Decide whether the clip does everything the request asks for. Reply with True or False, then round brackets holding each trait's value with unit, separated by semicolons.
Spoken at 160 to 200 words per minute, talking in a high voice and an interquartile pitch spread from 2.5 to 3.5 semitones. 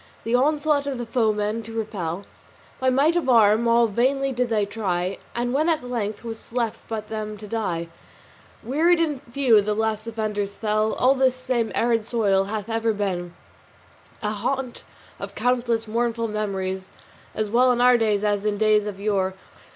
True (175 wpm; 225 Hz; 2.9 semitones)